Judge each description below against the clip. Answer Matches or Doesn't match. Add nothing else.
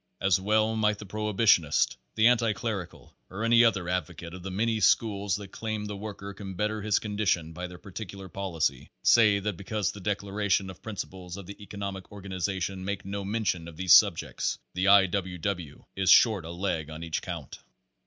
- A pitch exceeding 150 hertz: Doesn't match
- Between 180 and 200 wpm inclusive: Matches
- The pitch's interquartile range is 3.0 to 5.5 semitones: Doesn't match